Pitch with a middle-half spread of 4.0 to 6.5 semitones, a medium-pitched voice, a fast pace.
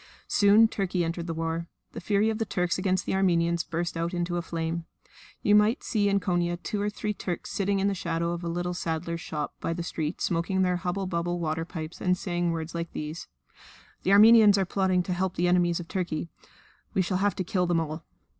No: narrow, 2.5 semitones; medium, 175 Hz; fast, 220 wpm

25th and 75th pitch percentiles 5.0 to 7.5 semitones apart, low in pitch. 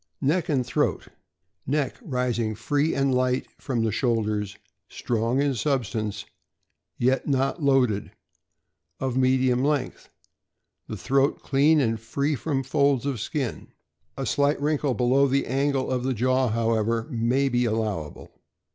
No: average, 3.1 semitones; low, 130 Hz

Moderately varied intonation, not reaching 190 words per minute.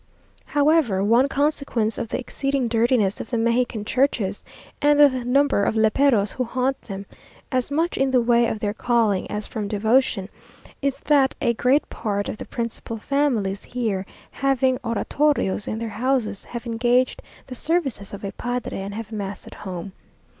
Yes: average, 4.2 semitones; average, 170 wpm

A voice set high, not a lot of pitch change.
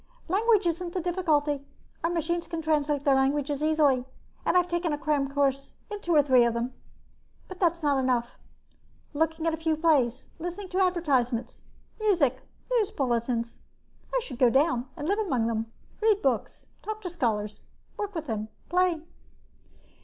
No: very high, 305 Hz; average, 5.2 semitones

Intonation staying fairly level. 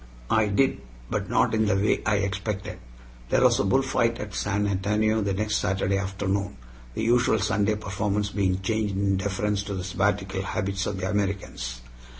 Yes: narrow, 1.7 semitones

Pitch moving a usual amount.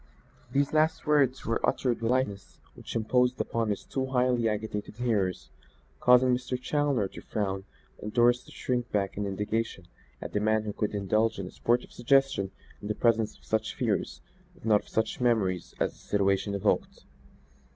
Yes: average, 3.3 semitones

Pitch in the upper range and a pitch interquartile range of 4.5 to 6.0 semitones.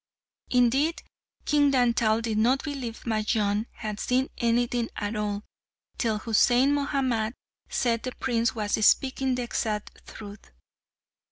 No: high, 235 Hz; average, 3.1 semitones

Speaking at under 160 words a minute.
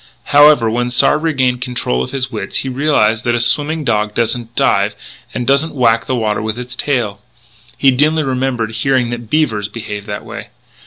No: average, 180 wpm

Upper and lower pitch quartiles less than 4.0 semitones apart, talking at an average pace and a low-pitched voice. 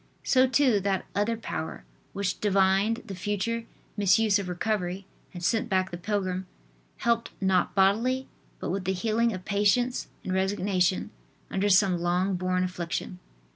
No: average, 2.8 semitones; average, 145 wpm; high, 195 Hz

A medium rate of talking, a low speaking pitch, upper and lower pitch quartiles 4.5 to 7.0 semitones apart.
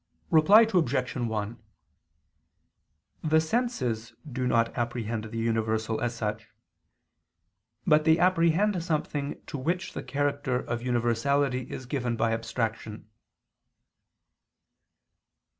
No: slow, 100 wpm; low, 125 Hz; average, 5.2 semitones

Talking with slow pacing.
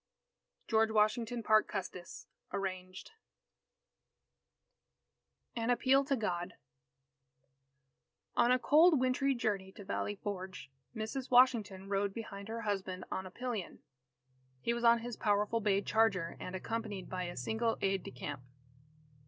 Yes: slow, 130 wpm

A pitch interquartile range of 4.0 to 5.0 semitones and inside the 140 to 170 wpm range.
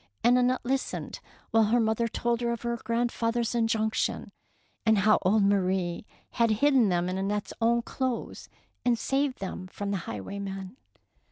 No: average, 3.1 semitones; average, 160 wpm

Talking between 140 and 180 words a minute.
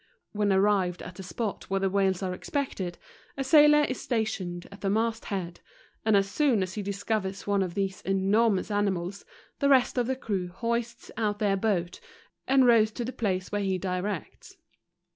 No: average, 195 wpm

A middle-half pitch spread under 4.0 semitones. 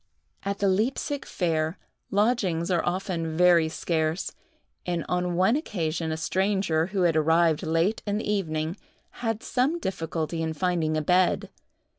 Yes: average, 3.6 semitones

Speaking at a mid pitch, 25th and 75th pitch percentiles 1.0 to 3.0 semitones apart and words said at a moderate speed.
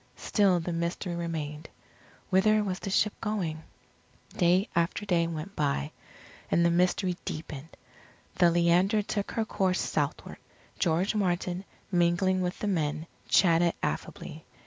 No: medium, 175 Hz; narrow, 2.4 semitones; slow, 130 wpm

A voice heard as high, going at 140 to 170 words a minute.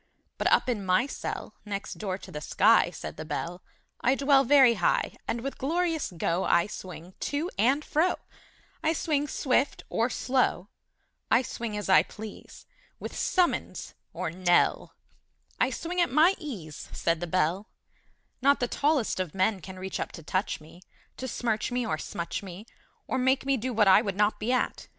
No: high, 220 Hz; average, 180 wpm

